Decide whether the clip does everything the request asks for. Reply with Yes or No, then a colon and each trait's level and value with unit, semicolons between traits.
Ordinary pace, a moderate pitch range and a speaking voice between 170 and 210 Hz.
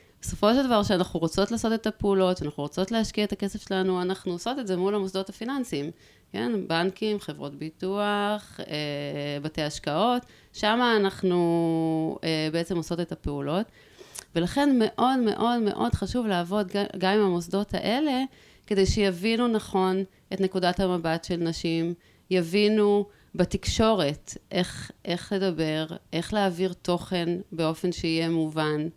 Yes: average, 130 wpm; average, 3.7 semitones; high, 190 Hz